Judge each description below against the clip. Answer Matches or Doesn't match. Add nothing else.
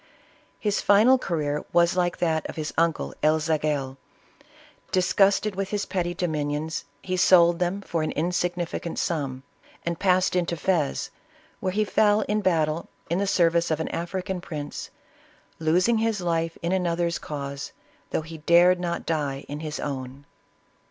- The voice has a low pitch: Doesn't match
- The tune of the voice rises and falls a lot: Doesn't match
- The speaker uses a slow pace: Doesn't match